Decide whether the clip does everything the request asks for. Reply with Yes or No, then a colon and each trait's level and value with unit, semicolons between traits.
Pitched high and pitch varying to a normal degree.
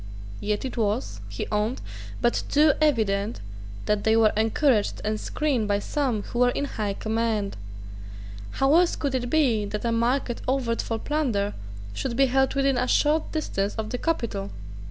Yes: high, 235 Hz; average, 4.2 semitones